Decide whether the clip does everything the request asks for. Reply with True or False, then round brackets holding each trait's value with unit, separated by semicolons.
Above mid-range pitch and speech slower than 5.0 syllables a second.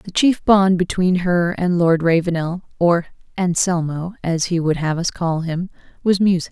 False (175 Hz; 4.4 syllables/s)